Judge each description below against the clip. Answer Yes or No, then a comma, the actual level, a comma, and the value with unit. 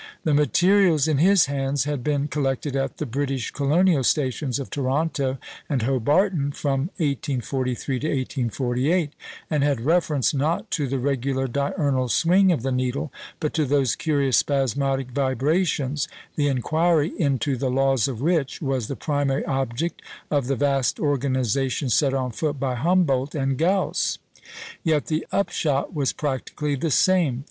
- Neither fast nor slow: Yes, average, 150 wpm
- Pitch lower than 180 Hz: Yes, medium, 140 Hz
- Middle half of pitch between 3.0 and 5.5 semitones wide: No, narrow, 2.5 semitones